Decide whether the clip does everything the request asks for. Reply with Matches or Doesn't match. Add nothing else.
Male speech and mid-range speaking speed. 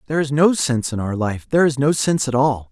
Doesn't match